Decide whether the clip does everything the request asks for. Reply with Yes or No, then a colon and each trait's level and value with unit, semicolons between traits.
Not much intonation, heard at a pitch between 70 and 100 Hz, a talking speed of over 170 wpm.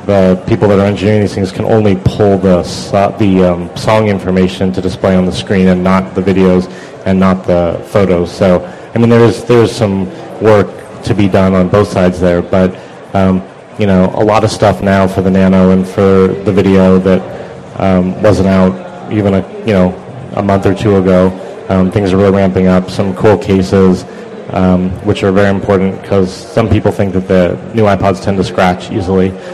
Yes: narrow, 1.5 semitones; very low, 95 Hz; average, 200 wpm